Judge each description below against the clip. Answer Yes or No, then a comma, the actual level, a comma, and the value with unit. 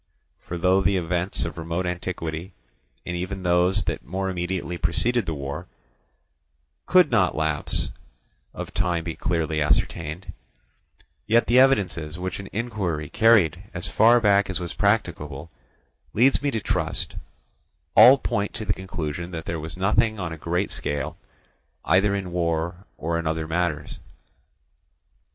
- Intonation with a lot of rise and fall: No, average, 3.3 semitones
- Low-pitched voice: Yes, very low, 90 Hz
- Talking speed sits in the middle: Yes, average, 145 wpm